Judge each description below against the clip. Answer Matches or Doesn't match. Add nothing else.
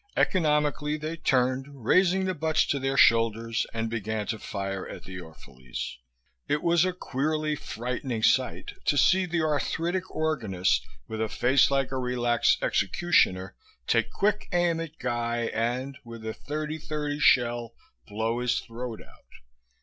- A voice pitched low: Matches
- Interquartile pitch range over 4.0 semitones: Matches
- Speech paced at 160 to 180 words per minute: Doesn't match